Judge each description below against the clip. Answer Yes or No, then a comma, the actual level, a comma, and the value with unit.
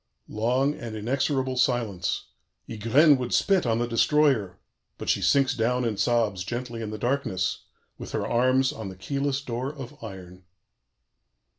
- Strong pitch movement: No, average, 3.6 semitones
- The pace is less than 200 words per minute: Yes, average, 150 wpm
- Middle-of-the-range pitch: No, low, 120 Hz